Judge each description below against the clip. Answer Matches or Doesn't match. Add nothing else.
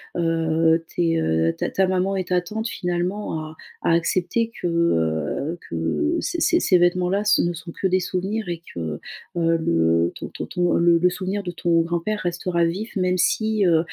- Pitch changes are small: Matches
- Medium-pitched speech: Matches